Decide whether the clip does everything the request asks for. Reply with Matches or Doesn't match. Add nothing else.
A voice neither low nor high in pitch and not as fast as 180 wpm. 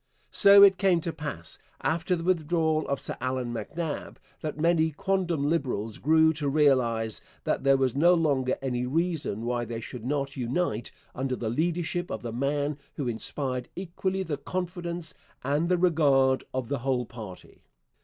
Matches